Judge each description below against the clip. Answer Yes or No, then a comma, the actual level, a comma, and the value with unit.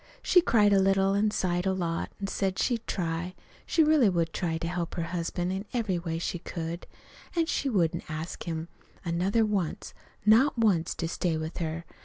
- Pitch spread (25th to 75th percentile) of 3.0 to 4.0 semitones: Yes, average, 3.7 semitones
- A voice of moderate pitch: Yes, medium, 180 Hz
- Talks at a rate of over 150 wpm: Yes, average, 190 wpm